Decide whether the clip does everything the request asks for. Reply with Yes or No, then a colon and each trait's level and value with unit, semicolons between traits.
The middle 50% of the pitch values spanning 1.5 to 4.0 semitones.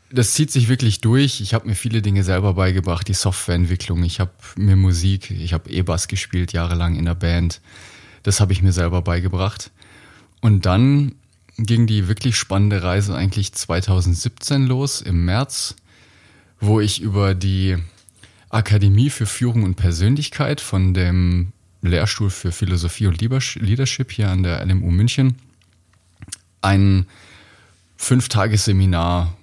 Yes: average, 3.4 semitones